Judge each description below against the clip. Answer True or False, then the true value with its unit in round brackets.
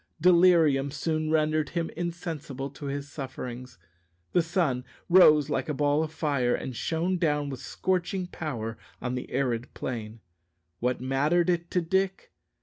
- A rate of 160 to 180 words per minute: False (145 wpm)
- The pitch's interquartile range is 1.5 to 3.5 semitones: False (4.3 semitones)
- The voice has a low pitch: False (150 Hz)